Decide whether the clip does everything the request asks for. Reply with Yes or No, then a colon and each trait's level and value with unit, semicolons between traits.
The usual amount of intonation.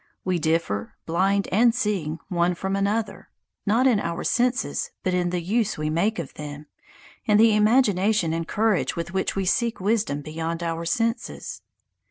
Yes: average, 4.6 semitones